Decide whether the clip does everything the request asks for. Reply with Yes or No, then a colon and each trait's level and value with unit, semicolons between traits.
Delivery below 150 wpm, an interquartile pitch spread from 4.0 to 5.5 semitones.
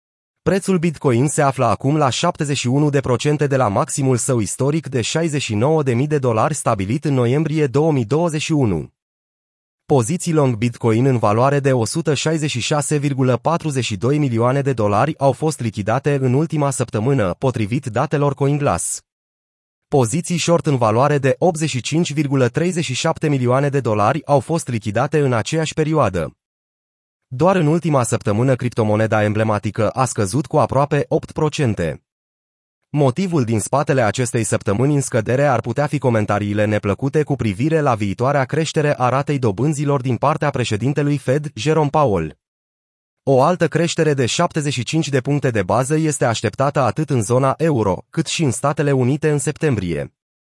Yes: average, 135 wpm; average, 4.6 semitones